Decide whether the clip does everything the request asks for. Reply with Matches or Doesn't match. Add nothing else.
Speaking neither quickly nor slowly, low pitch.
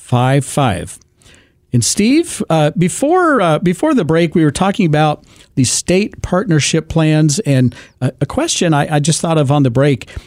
Doesn't match